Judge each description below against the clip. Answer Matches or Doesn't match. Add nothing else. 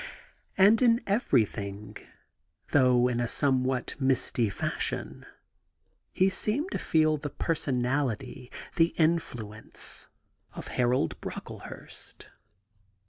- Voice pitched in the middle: Doesn't match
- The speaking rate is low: Matches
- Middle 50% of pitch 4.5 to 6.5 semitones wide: Matches